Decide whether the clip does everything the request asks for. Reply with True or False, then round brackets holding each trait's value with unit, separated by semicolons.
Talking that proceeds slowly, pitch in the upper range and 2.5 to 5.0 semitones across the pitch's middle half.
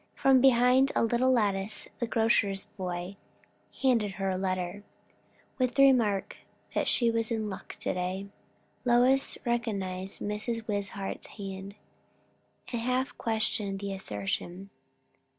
True (125 wpm; 210 Hz; 3.7 semitones)